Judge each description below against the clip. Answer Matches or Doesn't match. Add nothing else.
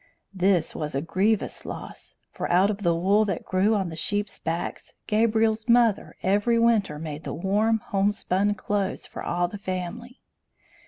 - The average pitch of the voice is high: Matches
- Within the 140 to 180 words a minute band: Matches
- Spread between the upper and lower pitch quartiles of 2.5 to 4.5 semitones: Matches